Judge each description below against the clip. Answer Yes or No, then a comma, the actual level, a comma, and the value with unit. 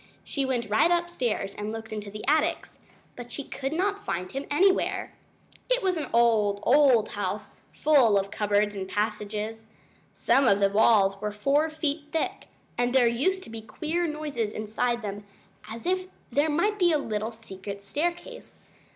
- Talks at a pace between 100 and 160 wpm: No, average, 170 wpm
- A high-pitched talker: Yes, high, 235 Hz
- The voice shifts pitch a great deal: Yes, wide, 6.6 semitones